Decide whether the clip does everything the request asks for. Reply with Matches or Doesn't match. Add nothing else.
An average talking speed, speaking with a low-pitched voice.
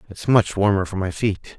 Doesn't match